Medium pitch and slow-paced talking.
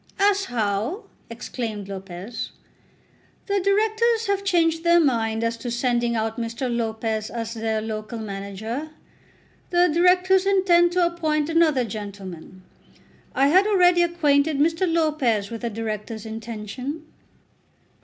No: very high, 250 Hz; slow, 125 wpm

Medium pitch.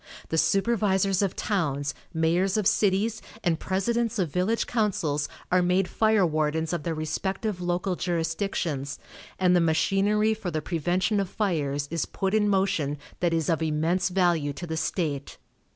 Yes: medium, 180 Hz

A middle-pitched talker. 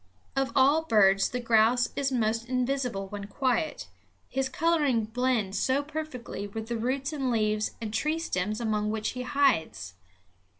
No: high, 240 Hz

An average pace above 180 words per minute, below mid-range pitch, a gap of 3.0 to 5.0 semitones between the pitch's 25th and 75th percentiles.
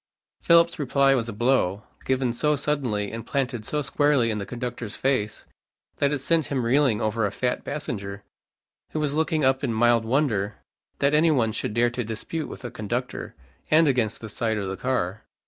Yes: average, 190 wpm; low, 125 Hz; average, 4.4 semitones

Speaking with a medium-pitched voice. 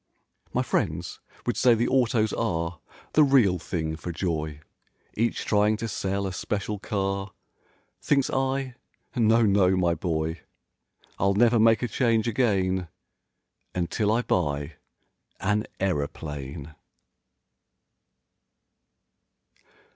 No: low, 100 Hz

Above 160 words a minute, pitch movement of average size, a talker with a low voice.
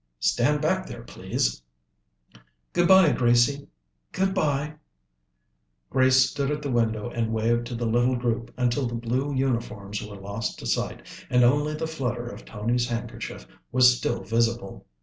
No: average, 150 wpm; average, 3.4 semitones; low, 120 Hz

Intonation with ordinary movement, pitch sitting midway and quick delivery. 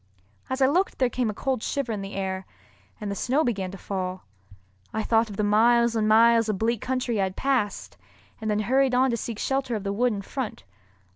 No: average, 3.6 semitones; high, 225 Hz; fast, 225 wpm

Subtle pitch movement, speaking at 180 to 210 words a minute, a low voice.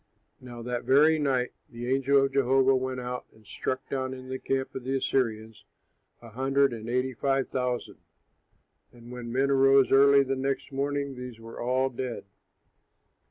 No: narrow, 1.6 semitones; average, 165 wpm; low, 130 Hz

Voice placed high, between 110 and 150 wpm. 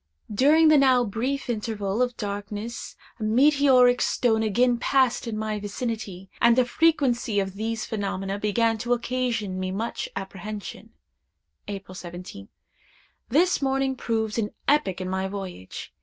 Yes: high, 225 Hz; average, 140 wpm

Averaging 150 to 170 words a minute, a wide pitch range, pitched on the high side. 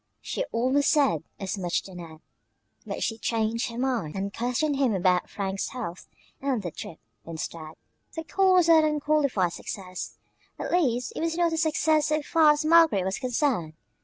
No: average, 180 wpm; wide, 8.2 semitones; high, 245 Hz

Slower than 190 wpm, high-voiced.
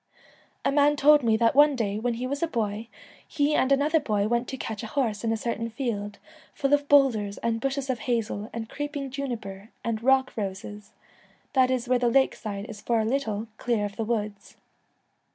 No: fast, 205 wpm; high, 235 Hz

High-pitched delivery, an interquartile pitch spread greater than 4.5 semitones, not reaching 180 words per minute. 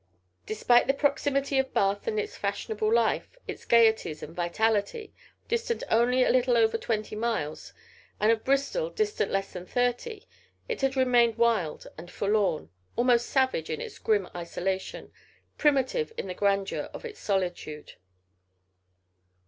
Yes: high, 230 Hz; average, 5.1 semitones; average, 140 wpm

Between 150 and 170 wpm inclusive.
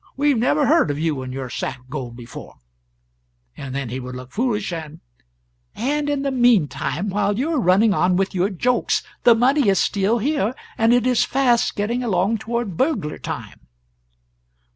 No: average, 185 wpm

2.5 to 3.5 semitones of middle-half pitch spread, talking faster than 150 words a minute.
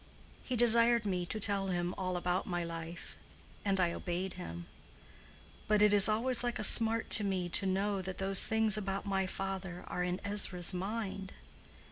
Yes: average, 2.8 semitones; average, 175 wpm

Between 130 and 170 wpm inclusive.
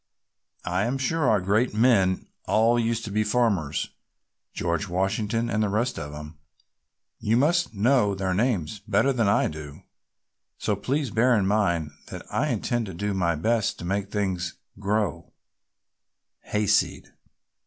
Yes: average, 150 wpm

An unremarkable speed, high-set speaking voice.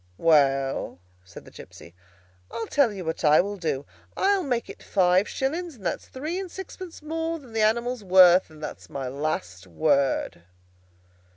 Yes: average, 165 wpm; high, 195 Hz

